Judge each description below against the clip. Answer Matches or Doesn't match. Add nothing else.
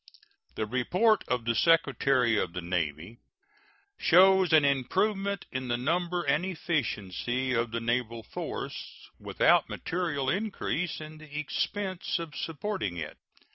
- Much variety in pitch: Matches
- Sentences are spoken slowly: Matches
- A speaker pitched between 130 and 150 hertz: Matches